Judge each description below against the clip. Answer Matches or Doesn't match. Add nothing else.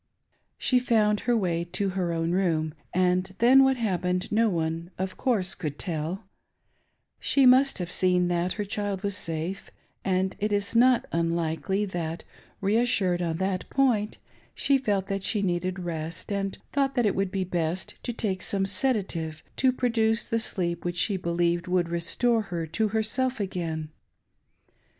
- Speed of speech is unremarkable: Matches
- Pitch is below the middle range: Doesn't match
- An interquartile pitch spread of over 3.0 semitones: Matches